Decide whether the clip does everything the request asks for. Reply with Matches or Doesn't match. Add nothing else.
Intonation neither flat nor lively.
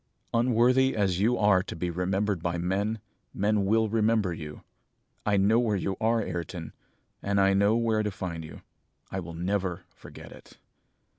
Matches